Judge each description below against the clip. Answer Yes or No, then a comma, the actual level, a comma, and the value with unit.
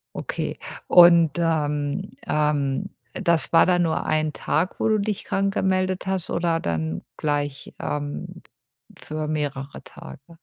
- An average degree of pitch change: Yes, average, 3.4 semitones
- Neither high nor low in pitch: Yes, medium, 160 Hz